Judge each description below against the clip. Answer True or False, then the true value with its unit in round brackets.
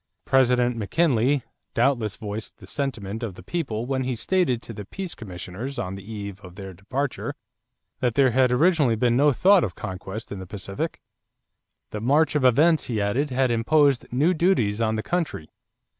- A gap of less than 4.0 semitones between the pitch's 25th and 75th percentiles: False (5.4 semitones)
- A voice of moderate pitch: False (120 Hz)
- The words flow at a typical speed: True (175 wpm)